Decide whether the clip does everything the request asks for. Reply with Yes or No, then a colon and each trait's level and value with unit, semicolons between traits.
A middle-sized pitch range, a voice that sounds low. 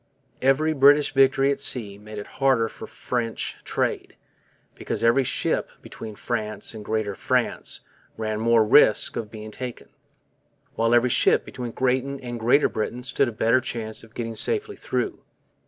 Yes: average, 3.3 semitones; low, 120 Hz